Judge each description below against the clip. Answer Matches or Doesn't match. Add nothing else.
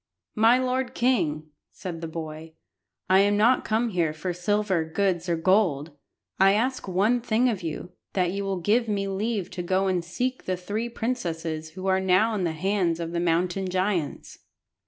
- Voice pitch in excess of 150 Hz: Matches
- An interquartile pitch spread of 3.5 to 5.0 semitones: Matches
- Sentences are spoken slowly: Doesn't match